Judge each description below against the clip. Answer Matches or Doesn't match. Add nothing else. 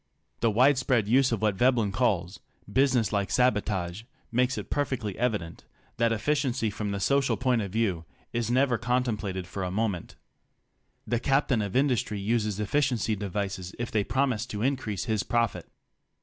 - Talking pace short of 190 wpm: Matches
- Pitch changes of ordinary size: Matches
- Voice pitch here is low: Matches